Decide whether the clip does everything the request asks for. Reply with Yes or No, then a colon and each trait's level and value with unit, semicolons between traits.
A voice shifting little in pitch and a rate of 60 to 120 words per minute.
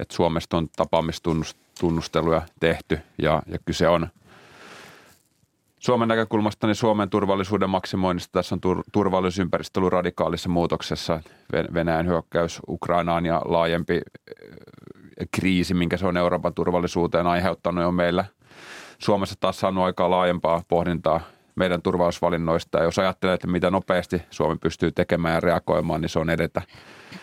No: narrow, 1.9 semitones; average, 130 wpm